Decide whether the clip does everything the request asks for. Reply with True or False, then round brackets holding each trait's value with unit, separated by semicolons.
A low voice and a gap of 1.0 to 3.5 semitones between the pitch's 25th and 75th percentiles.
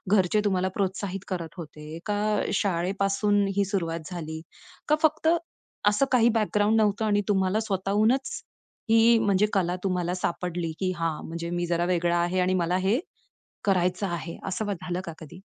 False (190 Hz; 3.0 semitones)